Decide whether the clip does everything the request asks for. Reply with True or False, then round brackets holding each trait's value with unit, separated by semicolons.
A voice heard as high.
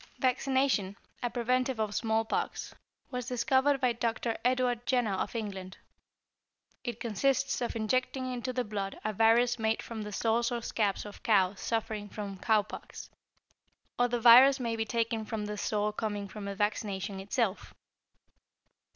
True (225 Hz)